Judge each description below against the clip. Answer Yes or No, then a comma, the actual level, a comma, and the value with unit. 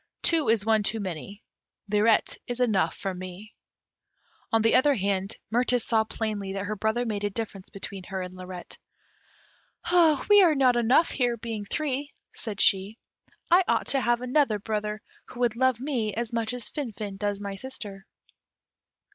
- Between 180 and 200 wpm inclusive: No, average, 165 wpm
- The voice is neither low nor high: No, high, 220 Hz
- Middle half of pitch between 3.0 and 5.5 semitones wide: Yes, average, 3.6 semitones